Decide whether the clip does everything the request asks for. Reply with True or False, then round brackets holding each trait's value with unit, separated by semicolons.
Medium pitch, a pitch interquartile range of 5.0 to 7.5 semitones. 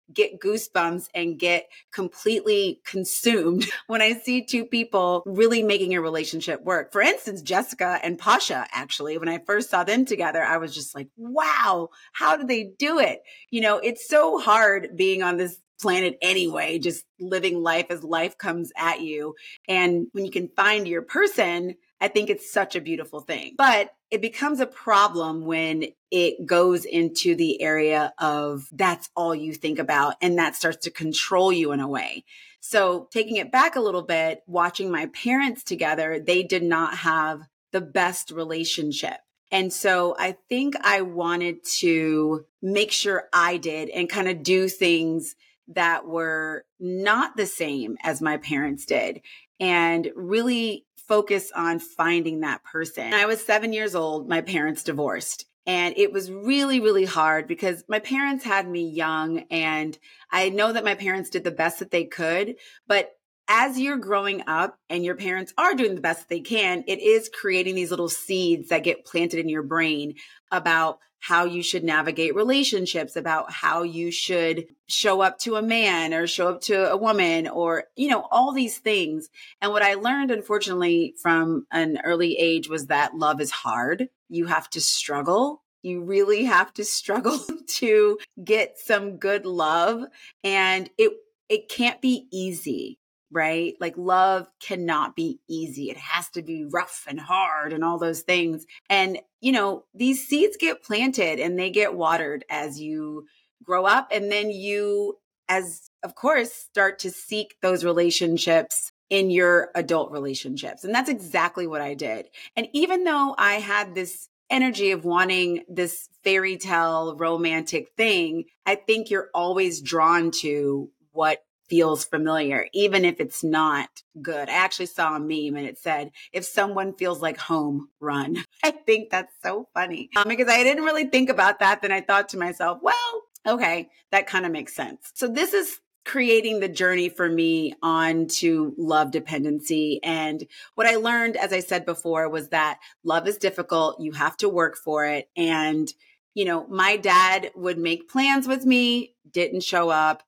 False (180 Hz; 4.5 semitones)